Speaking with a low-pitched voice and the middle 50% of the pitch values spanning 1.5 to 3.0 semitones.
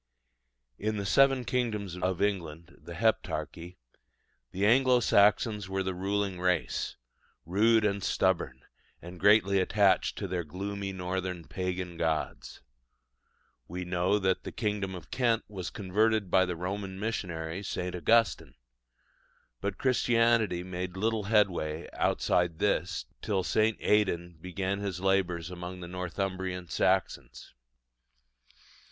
Yes: very low, 95 Hz; narrow, 2.6 semitones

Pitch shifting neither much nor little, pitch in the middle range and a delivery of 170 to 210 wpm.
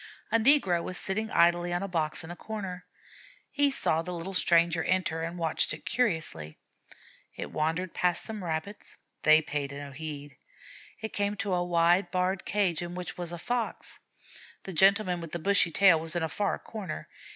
Yes: average, 3.3 semitones; medium, 175 Hz; average, 185 wpm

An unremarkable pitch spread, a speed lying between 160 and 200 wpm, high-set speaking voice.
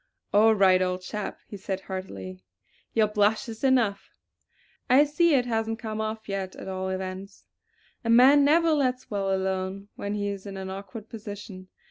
Yes: average, 3.0 semitones; average, 170 wpm; high, 205 Hz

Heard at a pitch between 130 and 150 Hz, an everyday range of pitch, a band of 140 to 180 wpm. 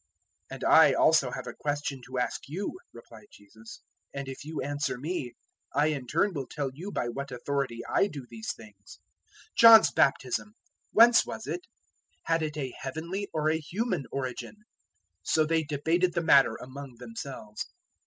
Yes: medium, 140 Hz; average, 4.5 semitones; average, 170 wpm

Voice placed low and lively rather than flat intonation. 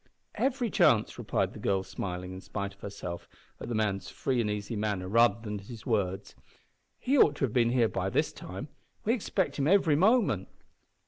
Yes: low, 110 Hz; wide, 6.4 semitones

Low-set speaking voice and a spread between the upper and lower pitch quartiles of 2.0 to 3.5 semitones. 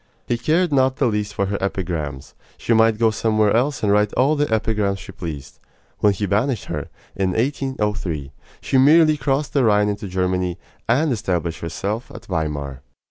No: low, 105 Hz; wide, 5.6 semitones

